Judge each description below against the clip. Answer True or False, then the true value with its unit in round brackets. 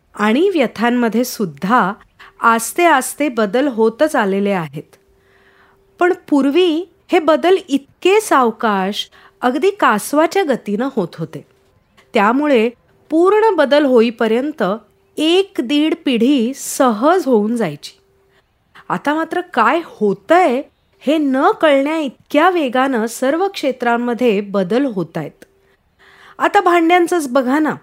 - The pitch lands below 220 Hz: False (265 Hz)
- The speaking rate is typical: True (105 wpm)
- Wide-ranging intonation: True (6.3 semitones)